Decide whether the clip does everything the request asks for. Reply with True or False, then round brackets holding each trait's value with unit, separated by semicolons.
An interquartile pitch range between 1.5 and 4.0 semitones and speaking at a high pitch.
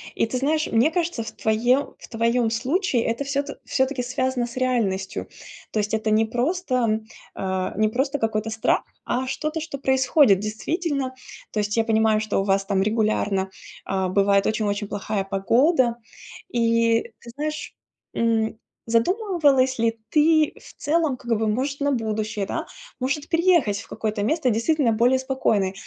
False (4.4 semitones; 235 Hz)